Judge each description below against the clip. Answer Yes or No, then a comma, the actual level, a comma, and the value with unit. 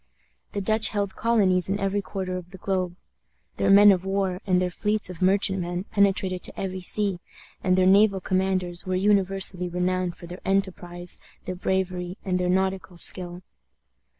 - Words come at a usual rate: Yes, average, 165 wpm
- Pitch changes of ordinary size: No, narrow, 1.4 semitones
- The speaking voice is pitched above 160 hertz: Yes, medium, 185 Hz